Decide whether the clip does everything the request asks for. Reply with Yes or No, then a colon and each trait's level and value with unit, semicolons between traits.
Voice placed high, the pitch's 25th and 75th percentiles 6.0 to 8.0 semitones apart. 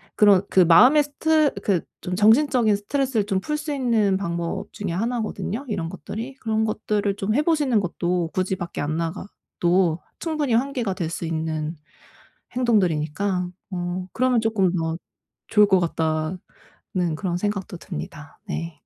No: high, 195 Hz; average, 5.2 semitones